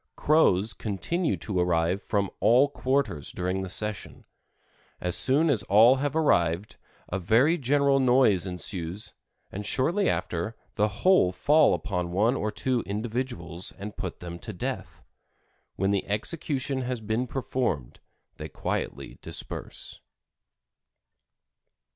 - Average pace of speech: No, slow, 125 wpm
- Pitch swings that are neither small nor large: No, wide, 6.2 semitones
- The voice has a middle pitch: No, low, 105 Hz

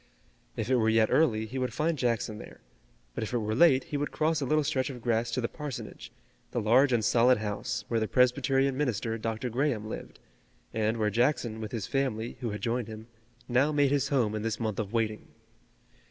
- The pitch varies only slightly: No, average, 3.3 semitones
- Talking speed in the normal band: No, fast, 210 wpm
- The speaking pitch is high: No, low, 120 Hz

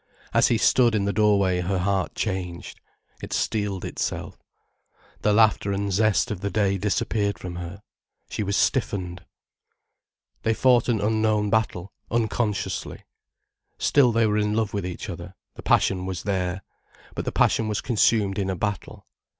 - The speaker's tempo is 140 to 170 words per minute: Yes, average, 160 wpm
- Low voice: Yes, low, 100 Hz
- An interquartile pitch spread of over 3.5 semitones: No, narrow, 2.4 semitones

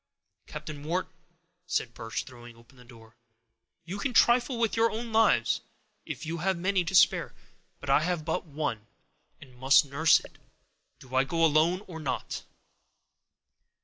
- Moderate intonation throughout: No, wide, 6.1 semitones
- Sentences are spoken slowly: No, average, 150 wpm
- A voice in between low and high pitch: Yes, medium, 155 Hz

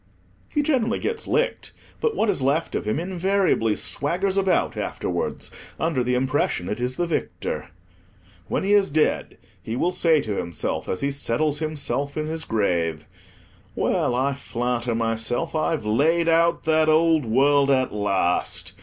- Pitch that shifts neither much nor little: No, wide, 6.3 semitones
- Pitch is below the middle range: No, medium, 145 Hz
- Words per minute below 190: Yes, average, 155 wpm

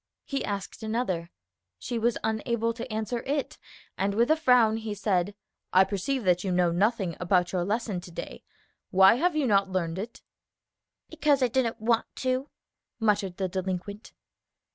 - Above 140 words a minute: Yes, average, 165 wpm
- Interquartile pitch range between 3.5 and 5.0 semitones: Yes, average, 4.1 semitones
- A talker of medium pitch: No, high, 215 Hz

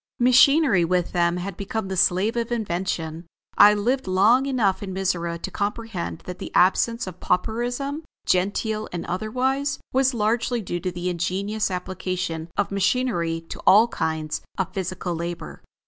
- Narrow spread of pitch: No, average, 4.6 semitones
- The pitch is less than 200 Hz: Yes, high, 190 Hz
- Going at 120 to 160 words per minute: Yes, average, 150 wpm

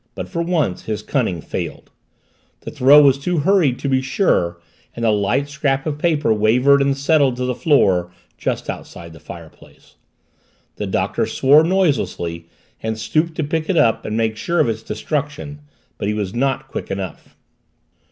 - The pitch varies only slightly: No, wide, 5.6 semitones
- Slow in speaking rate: No, average, 170 wpm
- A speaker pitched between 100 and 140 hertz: Yes, low, 135 Hz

